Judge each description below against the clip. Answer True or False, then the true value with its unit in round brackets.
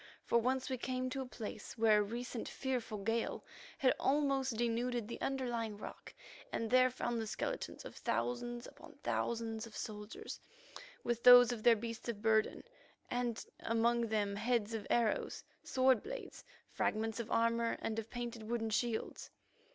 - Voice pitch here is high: True (235 Hz)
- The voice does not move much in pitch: True (1.8 semitones)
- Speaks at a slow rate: False (160 wpm)